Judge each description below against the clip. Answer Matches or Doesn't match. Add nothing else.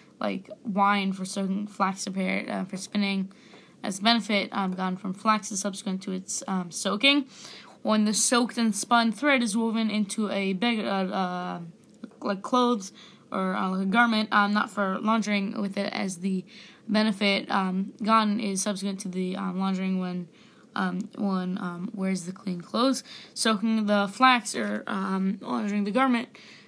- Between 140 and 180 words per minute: Matches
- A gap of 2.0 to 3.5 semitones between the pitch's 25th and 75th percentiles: Matches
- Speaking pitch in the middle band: Doesn't match